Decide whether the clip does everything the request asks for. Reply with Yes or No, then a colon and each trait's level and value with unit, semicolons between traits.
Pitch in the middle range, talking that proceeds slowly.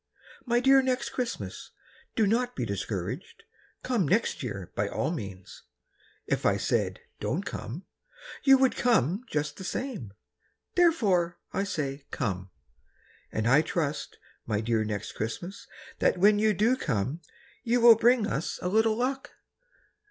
No: medium, 180 Hz; average, 145 wpm